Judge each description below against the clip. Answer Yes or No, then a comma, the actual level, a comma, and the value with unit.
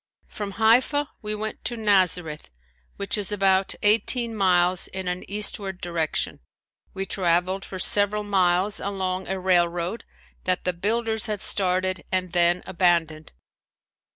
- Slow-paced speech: Yes, slow, 130 wpm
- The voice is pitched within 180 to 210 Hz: Yes, high, 190 Hz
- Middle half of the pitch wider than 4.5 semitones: No, narrow, 2.6 semitones